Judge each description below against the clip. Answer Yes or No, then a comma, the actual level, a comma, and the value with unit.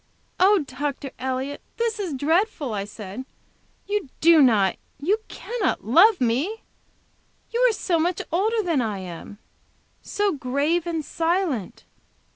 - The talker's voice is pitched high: Yes, very high, 315 Hz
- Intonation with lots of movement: Yes, wide, 7.3 semitones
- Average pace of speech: No, slow, 130 wpm